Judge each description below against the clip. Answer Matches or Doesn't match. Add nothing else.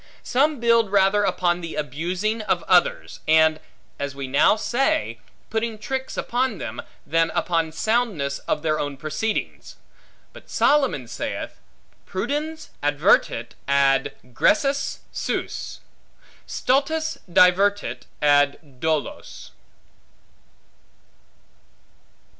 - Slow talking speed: Matches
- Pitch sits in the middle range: Matches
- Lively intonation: Matches